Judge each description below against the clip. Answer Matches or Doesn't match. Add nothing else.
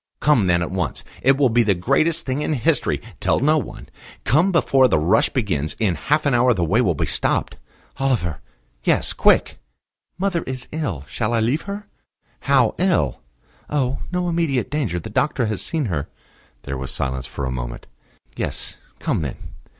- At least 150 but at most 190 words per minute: Matches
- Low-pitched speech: Matches